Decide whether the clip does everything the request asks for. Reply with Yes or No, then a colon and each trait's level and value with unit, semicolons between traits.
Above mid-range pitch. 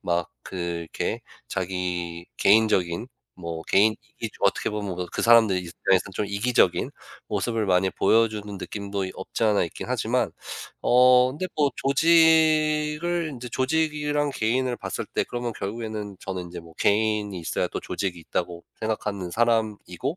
No: low, 105 Hz